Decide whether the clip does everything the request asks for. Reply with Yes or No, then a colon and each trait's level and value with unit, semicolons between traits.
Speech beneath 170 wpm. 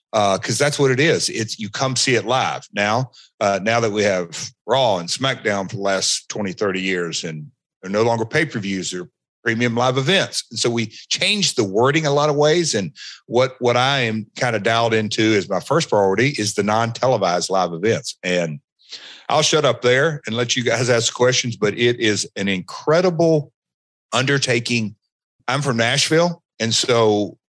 No: average, 195 wpm